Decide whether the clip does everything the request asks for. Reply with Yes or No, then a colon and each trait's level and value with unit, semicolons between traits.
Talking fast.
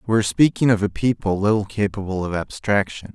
No: average, 190 wpm